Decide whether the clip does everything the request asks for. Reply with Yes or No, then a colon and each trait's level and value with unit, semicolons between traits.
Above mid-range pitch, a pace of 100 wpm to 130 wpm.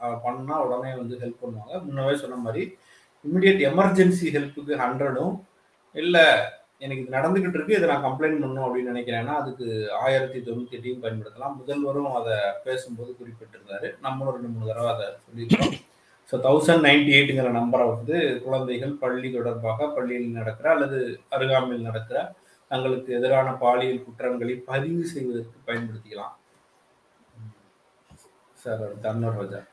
No: low, 130 Hz; average, 125 wpm